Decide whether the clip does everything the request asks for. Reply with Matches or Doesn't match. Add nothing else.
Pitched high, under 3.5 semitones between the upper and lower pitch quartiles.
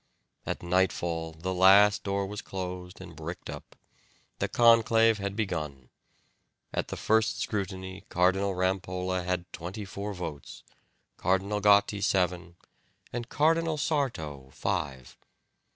Doesn't match